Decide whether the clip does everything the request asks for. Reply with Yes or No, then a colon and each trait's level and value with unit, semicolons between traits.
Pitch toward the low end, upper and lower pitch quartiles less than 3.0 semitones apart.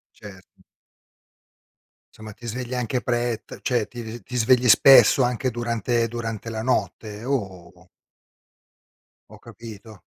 Yes: low, 115 Hz; narrow, 2.4 semitones